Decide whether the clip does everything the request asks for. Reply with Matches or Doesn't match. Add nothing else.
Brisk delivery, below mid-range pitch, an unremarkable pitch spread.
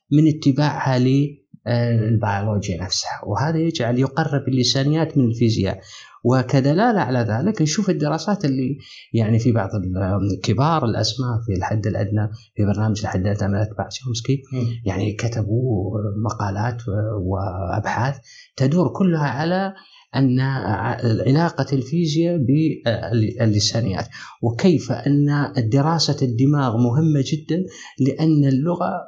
Doesn't match